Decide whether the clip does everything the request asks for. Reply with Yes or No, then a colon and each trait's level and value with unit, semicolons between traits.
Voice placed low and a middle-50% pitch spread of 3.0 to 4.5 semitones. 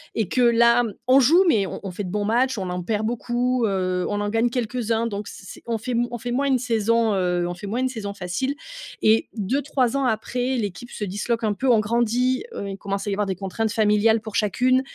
No: high, 225 Hz; average, 3.3 semitones